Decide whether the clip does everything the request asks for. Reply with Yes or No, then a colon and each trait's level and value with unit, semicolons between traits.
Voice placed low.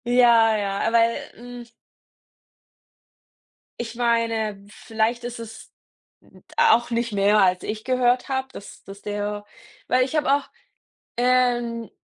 No: high, 230 Hz